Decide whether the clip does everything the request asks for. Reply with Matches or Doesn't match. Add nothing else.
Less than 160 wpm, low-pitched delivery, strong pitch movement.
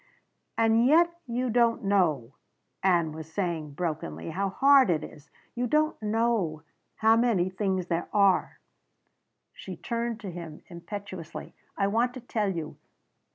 Doesn't match